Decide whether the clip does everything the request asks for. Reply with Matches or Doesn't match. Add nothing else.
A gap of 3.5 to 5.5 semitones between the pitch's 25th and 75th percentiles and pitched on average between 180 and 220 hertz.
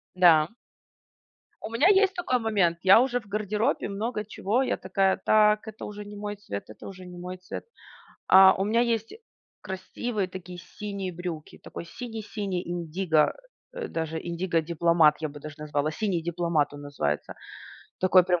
Matches